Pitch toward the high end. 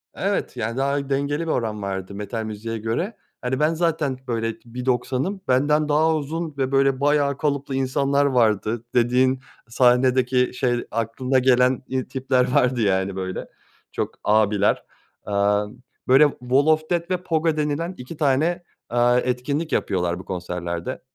No: low, 130 Hz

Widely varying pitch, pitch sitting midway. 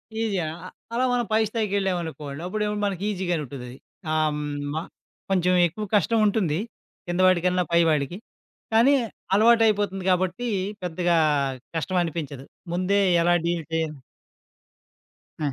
No: average, 4.1 semitones; medium, 180 Hz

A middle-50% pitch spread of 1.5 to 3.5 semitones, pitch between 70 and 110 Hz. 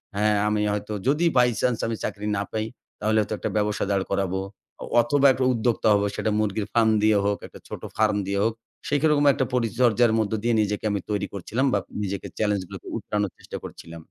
Yes: narrow, 2.5 semitones; low, 105 Hz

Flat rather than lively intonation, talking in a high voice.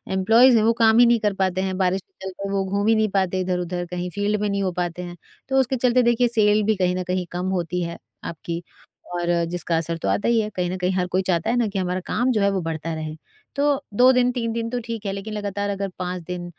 No: average, 3.8 semitones; high, 195 Hz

